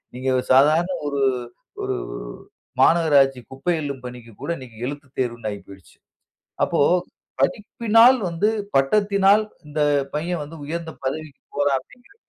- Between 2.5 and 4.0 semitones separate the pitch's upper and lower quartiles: No, average, 4.8 semitones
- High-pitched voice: No, medium, 145 Hz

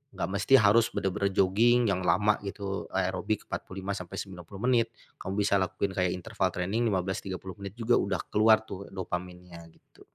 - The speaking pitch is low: Yes, low, 100 Hz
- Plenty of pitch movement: No, narrow, 2.4 semitones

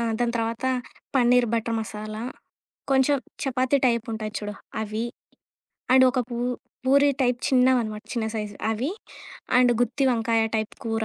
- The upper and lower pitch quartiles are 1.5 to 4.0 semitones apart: Yes, narrow, 2.4 semitones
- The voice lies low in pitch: No, high, 235 Hz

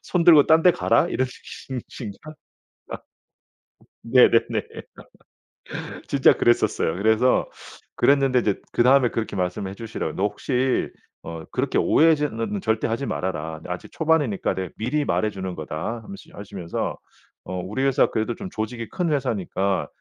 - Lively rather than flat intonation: Yes, wide, 5.8 semitones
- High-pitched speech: No, low, 115 Hz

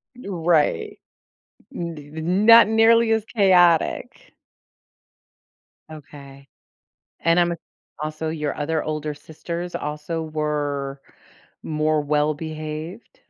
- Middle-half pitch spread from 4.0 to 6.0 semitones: No, average, 2.7 semitones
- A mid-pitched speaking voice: Yes, medium, 155 Hz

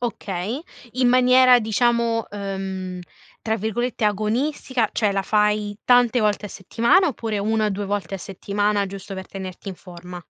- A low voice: No, high, 210 Hz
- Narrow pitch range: No, average, 3.3 semitones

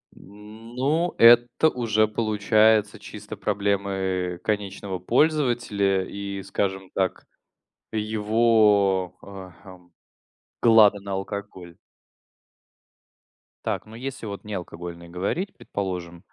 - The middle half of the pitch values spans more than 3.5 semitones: No, average, 2.7 semitones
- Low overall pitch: Yes, low, 100 Hz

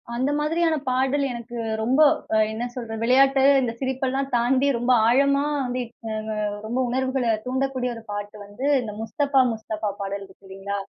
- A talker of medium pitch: No, very high, 250 Hz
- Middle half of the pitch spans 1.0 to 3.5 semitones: Yes, average, 3.2 semitones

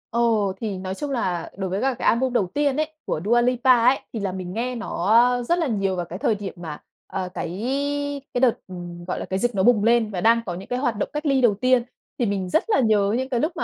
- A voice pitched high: Yes, high, 225 Hz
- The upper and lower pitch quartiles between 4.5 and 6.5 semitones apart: Yes, average, 4.9 semitones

